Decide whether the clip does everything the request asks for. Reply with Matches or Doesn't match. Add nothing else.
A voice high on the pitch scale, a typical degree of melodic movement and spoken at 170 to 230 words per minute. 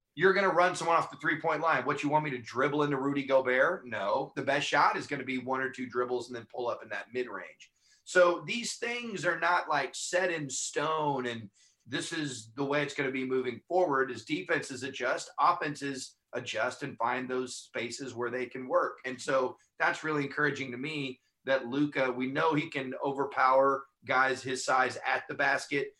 Doesn't match